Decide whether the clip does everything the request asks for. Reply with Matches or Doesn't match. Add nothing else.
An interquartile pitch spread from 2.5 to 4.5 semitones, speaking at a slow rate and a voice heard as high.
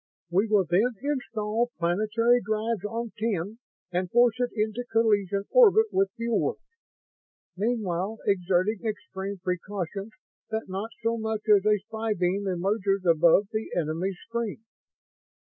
Matches